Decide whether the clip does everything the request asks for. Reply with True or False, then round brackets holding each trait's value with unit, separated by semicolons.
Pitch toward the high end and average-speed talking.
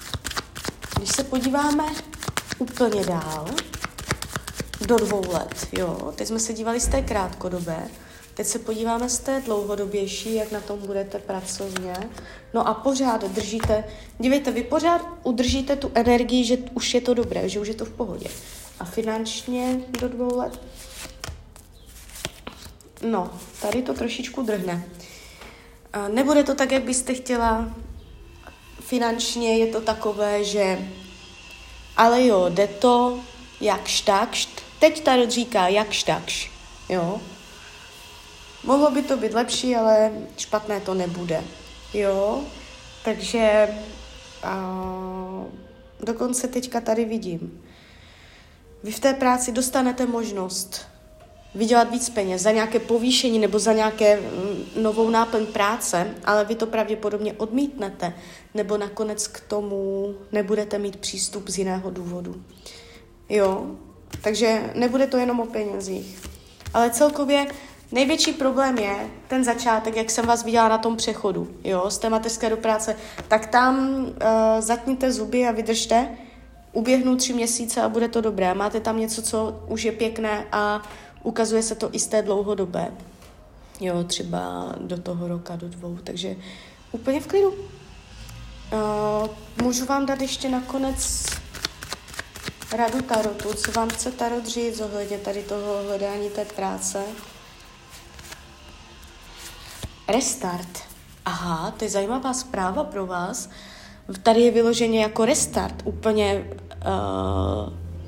True (220 Hz; 130 wpm)